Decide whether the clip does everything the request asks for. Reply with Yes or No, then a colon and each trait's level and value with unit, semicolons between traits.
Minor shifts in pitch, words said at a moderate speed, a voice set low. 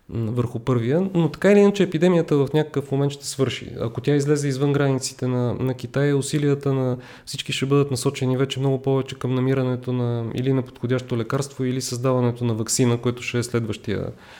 No: narrow, 2.2 semitones; fast, 185 wpm; low, 130 Hz